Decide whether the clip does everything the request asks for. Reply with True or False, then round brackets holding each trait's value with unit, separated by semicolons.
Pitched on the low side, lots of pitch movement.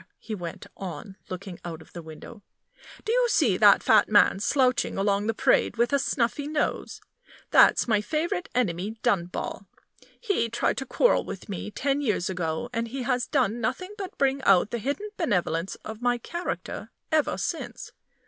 False (230 Hz; 6.3 semitones)